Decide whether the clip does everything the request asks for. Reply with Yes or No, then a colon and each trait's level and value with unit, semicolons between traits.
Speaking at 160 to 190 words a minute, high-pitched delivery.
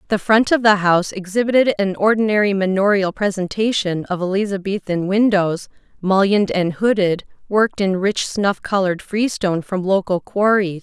No: average, 140 wpm; high, 195 Hz